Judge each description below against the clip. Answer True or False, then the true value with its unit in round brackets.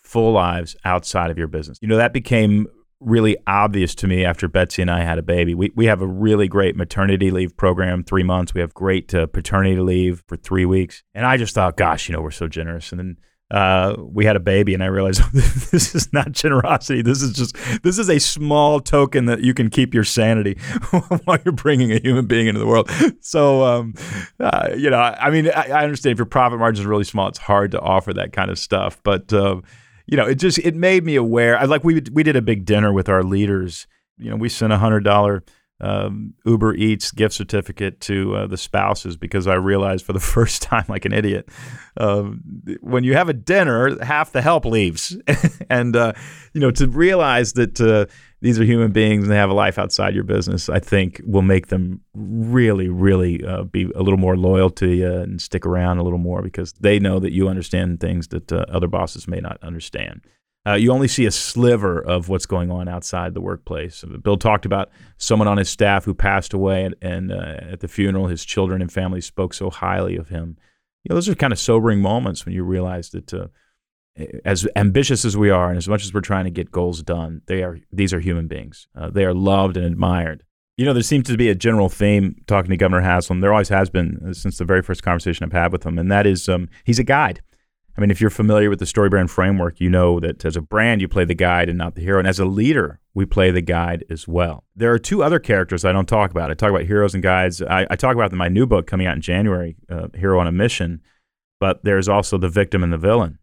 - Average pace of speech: False (240 wpm)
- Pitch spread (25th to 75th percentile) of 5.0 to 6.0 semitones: False (4.0 semitones)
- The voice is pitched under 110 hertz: True (100 Hz)